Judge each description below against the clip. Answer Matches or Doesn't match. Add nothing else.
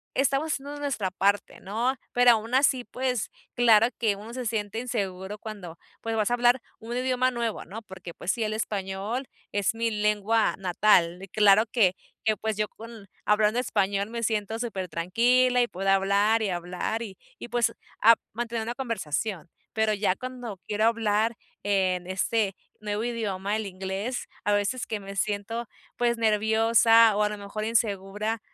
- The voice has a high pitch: Matches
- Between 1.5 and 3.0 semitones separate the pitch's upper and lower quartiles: Matches